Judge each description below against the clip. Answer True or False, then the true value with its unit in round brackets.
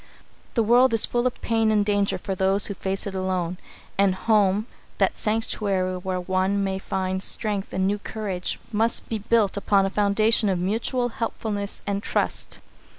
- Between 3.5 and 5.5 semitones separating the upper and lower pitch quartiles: False (2.4 semitones)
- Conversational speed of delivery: True (170 wpm)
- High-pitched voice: True (200 Hz)